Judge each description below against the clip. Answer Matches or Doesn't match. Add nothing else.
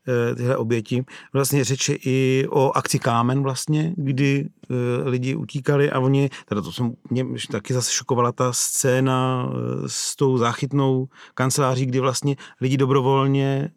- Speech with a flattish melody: Matches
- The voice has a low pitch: Matches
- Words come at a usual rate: Matches